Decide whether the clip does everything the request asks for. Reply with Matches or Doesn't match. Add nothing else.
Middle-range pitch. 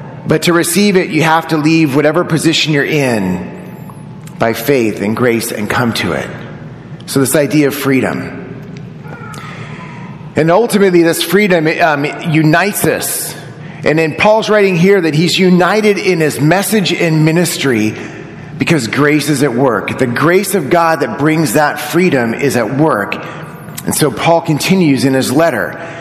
Matches